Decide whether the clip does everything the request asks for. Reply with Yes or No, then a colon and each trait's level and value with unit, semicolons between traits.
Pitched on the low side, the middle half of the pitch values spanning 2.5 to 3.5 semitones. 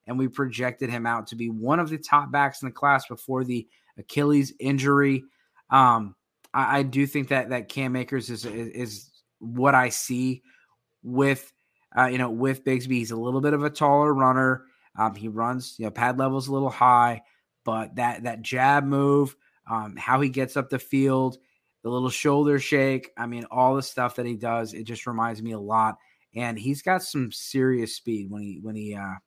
Yes: low, 130 Hz; average, 2.8 semitones